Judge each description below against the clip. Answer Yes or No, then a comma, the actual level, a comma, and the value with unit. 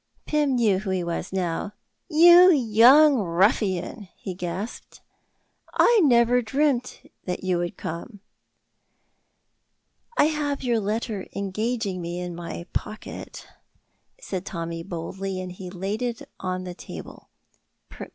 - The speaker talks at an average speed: No, slow, 120 wpm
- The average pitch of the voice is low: No, high, 200 Hz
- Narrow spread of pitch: No, wide, 5.5 semitones